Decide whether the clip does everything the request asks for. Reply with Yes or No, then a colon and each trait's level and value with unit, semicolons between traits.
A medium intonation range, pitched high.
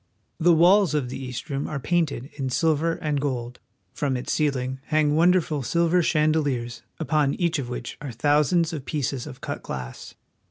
No: average, 3.9 semitones; medium, 145 Hz